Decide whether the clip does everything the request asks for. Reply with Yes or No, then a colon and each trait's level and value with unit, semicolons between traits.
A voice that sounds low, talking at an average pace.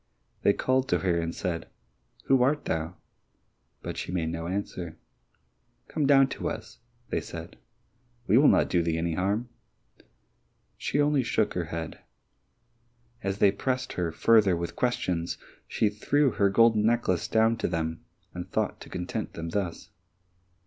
Yes: very low, 95 Hz; average, 155 wpm